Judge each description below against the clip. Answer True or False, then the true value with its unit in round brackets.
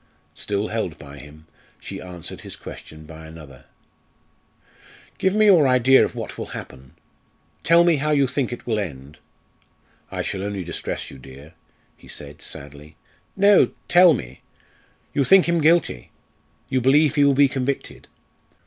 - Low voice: True (115 Hz)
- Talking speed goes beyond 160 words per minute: False (155 wpm)